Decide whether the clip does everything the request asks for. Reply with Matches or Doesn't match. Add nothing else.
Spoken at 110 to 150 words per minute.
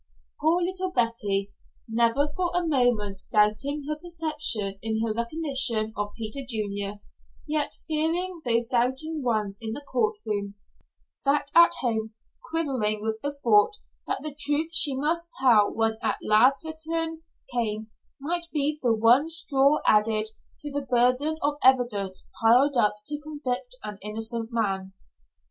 Matches